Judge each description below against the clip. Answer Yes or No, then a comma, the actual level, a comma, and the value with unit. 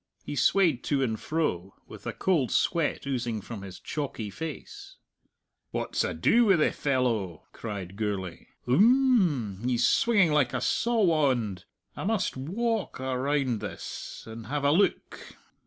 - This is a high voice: No, low, 135 Hz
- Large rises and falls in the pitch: Yes, wide, 7.2 semitones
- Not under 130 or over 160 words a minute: Yes, average, 145 wpm